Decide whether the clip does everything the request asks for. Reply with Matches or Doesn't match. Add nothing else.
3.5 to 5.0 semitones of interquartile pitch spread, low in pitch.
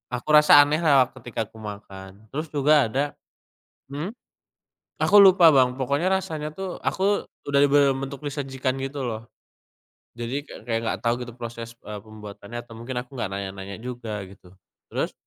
Matches